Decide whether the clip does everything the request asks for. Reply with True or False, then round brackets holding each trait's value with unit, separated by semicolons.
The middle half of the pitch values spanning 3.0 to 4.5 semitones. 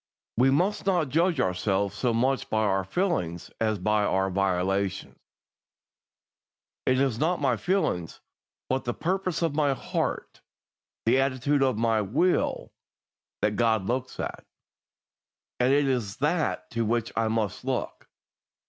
False (5.6 semitones)